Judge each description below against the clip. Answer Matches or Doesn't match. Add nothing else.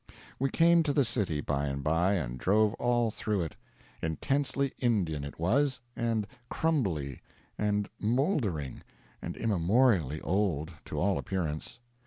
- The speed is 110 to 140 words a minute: Matches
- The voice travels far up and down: Matches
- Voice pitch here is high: Doesn't match